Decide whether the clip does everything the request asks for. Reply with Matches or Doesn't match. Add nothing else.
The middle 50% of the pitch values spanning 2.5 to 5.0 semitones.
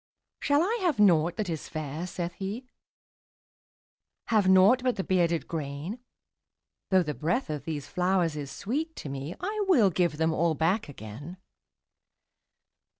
Doesn't match